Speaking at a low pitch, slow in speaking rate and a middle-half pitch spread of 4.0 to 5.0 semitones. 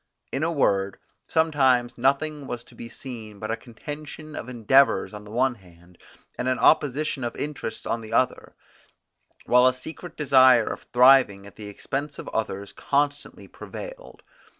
No: low, 130 Hz; average, 160 wpm; average, 4.5 semitones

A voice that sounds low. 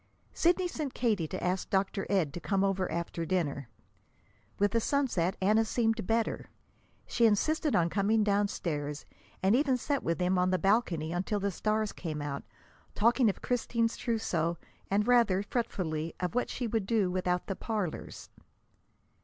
No: high, 200 Hz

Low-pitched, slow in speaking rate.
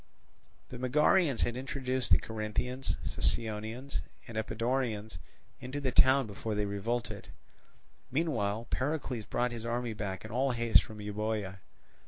Yes: low, 115 Hz; slow, 130 wpm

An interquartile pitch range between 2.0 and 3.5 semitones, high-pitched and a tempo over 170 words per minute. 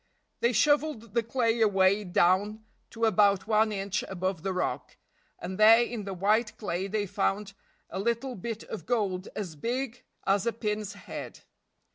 No: average, 3.0 semitones; high, 210 Hz; average, 160 wpm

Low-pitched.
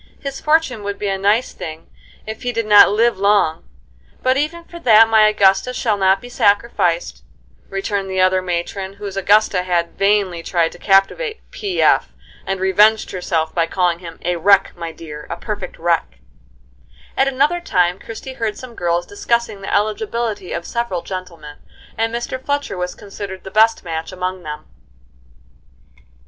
No: high, 195 Hz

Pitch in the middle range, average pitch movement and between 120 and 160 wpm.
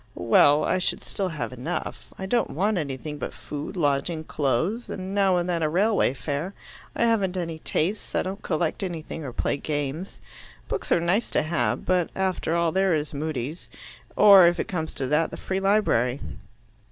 No: medium, 170 Hz; average, 4.4 semitones; average, 185 wpm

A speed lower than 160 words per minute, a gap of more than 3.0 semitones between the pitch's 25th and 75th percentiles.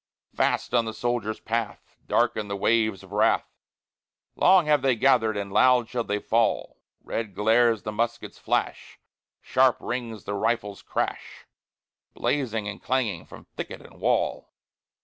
No: average, 145 wpm; narrow, 2.6 semitones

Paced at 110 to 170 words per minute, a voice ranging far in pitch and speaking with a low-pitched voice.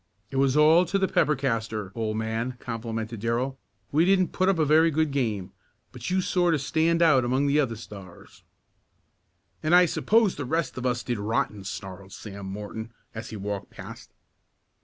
No: average, 180 wpm; wide, 6.3 semitones; low, 125 Hz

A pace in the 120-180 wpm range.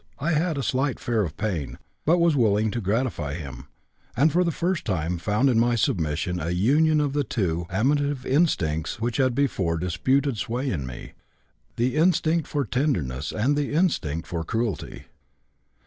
Yes: average, 170 wpm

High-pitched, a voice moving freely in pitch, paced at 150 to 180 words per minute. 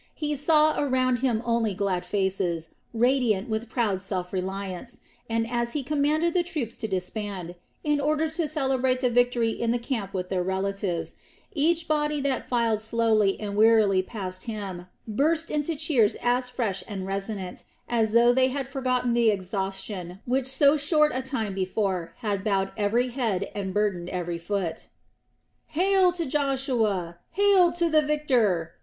Yes: high, 230 Hz; wide, 5.8 semitones; average, 160 wpm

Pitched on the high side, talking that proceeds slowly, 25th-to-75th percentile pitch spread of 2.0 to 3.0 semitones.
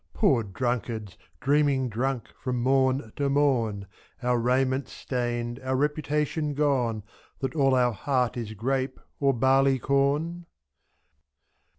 No: low, 130 Hz; slow, 120 wpm; narrow, 2.6 semitones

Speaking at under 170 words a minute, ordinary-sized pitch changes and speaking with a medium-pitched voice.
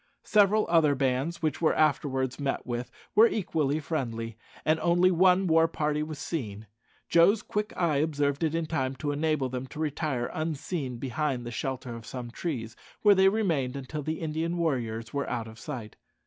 No: average, 175 wpm; average, 4.2 semitones; medium, 150 Hz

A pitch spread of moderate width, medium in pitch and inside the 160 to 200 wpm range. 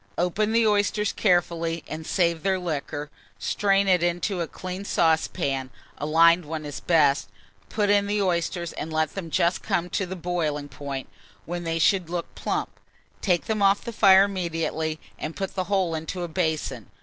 Yes: average, 3.3 semitones; medium, 175 Hz; average, 175 wpm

